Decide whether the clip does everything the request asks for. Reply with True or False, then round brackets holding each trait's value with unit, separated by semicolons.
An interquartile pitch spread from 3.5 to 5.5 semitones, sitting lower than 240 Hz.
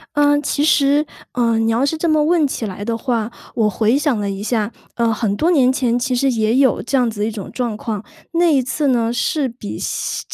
False (4.2 semitones; 245 Hz)